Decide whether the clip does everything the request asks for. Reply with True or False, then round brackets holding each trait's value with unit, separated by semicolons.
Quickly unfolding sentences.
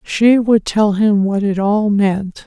False (195 wpm)